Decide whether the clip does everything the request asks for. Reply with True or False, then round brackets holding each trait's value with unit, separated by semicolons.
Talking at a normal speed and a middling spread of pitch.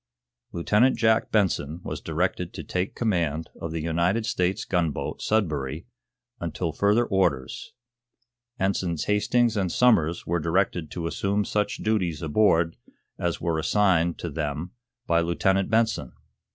False (130 wpm; 4.0 semitones)